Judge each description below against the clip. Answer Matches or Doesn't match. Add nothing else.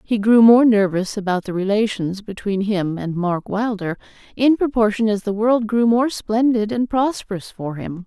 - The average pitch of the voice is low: Doesn't match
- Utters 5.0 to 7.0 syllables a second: Doesn't match